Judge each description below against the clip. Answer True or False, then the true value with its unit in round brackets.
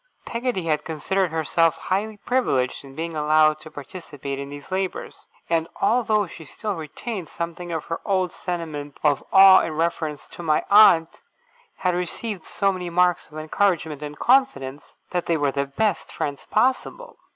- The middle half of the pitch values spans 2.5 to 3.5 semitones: False (4.1 semitones)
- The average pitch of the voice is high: False (170 Hz)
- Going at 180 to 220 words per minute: False (160 wpm)